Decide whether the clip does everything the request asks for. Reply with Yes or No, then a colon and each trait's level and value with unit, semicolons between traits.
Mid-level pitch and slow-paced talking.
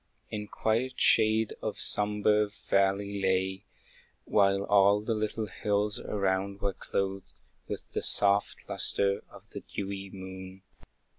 No: low, 100 Hz; slow, 125 wpm